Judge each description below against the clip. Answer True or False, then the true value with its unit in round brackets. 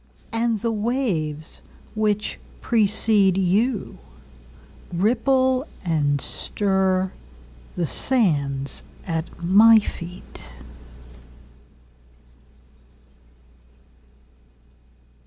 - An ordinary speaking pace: False (45 wpm)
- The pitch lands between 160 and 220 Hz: True (190 Hz)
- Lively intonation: True (6.5 semitones)